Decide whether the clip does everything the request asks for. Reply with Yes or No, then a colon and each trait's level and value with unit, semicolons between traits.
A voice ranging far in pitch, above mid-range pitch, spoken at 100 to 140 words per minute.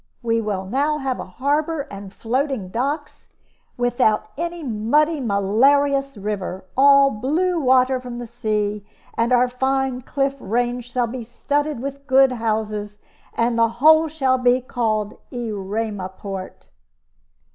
No: average, 4.3 semitones; high, 245 Hz; slow, 135 wpm